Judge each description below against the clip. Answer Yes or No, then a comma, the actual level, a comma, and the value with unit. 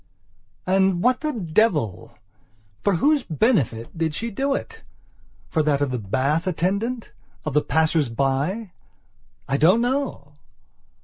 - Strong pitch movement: Yes, wide, 8.0 semitones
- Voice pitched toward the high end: No, medium, 175 Hz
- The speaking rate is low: Yes, slow, 130 wpm